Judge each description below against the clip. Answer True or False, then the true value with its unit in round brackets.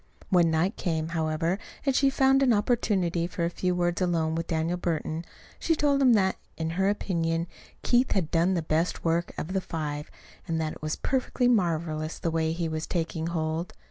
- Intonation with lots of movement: False (3.0 semitones)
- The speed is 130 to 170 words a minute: False (195 wpm)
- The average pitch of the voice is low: False (170 Hz)